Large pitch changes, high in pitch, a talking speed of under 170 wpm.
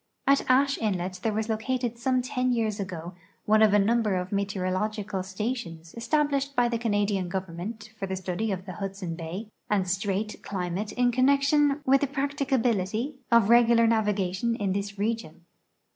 No: average, 4.1 semitones; high, 215 Hz; average, 160 wpm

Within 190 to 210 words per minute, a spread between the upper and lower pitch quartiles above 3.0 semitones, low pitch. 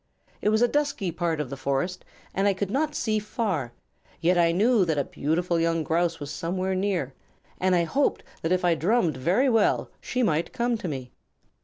No: average, 200 wpm; average, 4.7 semitones; medium, 180 Hz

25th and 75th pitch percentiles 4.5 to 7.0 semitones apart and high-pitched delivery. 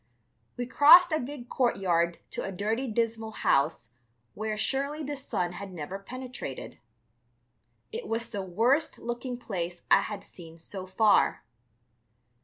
Yes: wide, 5.6 semitones; high, 220 Hz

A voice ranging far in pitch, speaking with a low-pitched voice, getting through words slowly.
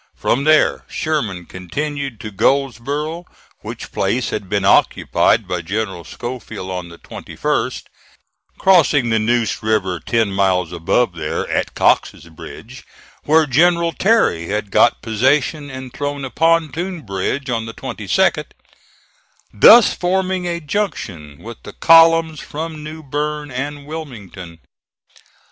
Yes: wide, 7.5 semitones; low, 130 Hz; slow, 125 wpm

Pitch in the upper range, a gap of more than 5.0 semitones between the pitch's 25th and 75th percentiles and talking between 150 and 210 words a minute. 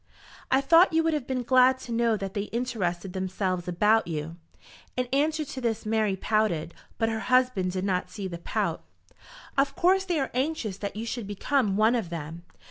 Yes: high, 220 Hz; wide, 5.5 semitones; average, 195 wpm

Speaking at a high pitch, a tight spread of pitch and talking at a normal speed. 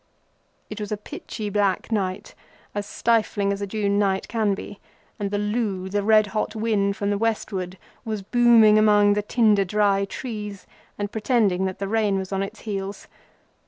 Yes: high, 205 Hz; narrow, 1.5 semitones; average, 175 wpm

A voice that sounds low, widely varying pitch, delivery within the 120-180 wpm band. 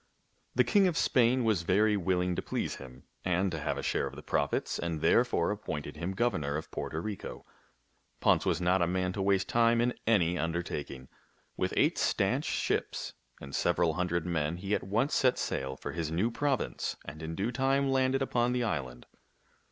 No: very low, 95 Hz; wide, 6.4 semitones; average, 190 wpm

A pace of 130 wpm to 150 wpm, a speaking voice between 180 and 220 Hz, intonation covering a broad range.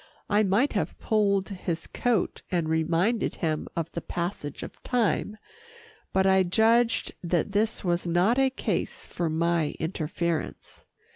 No: average, 140 wpm; medium, 185 Hz; average, 4.3 semitones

